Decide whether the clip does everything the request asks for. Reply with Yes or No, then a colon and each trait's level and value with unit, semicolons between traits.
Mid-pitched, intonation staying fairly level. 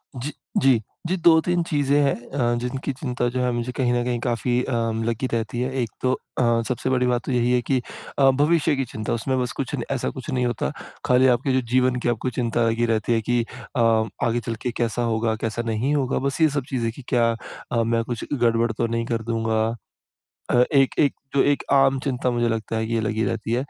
No: low, 120 Hz; narrow, 2.2 semitones